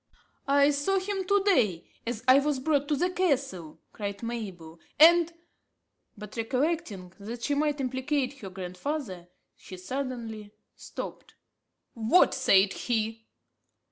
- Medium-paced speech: No, slow, 130 wpm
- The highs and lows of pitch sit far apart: Yes, wide, 6.2 semitones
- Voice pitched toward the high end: Yes, very high, 255 Hz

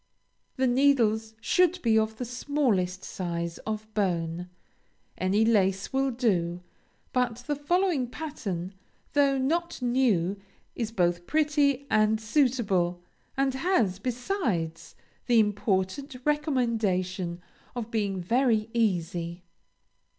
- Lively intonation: Yes, wide, 6.2 semitones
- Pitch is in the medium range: No, high, 220 Hz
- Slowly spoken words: Yes, slow, 105 wpm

